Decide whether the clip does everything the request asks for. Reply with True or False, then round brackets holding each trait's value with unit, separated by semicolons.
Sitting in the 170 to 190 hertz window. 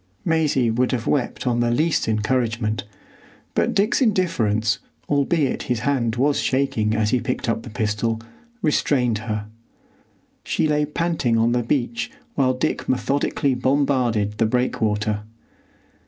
False (125 Hz)